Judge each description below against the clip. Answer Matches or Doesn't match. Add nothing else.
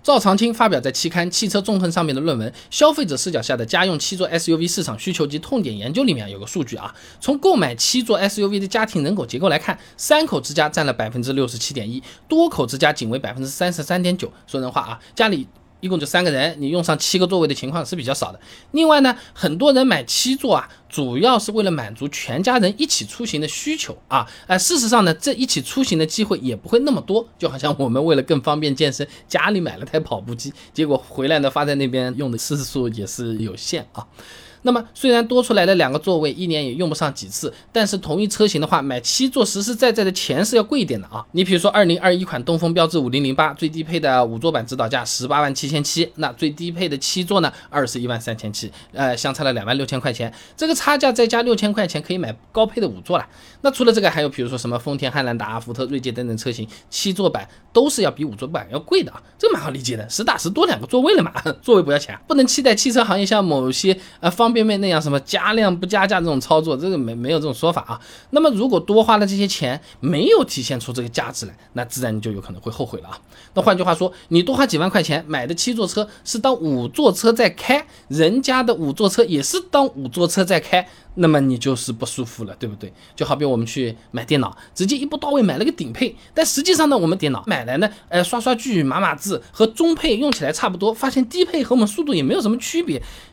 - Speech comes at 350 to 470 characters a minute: Matches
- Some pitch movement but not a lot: Doesn't match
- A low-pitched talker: Doesn't match